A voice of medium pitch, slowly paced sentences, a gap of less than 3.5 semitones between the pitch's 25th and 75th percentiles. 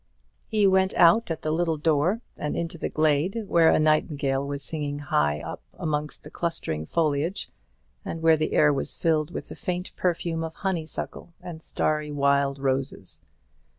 No: medium, 155 Hz; average, 165 wpm; average, 2.8 semitones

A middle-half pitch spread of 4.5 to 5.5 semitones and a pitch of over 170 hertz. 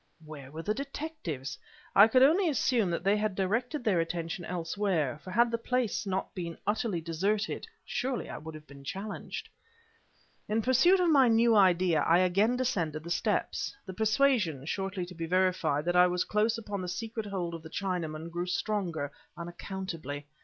Yes: average, 5.0 semitones; high, 190 Hz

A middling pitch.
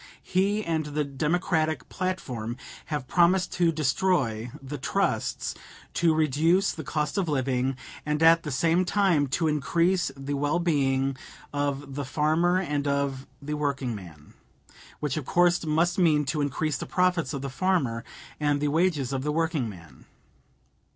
Yes: medium, 150 Hz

